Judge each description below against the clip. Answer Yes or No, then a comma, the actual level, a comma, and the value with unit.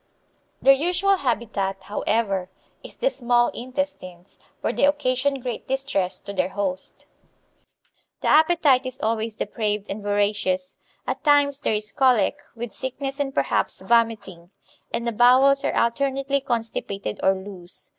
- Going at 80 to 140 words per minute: Yes, slow, 135 wpm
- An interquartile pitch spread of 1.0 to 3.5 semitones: No, average, 5.2 semitones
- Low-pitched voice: No, high, 235 Hz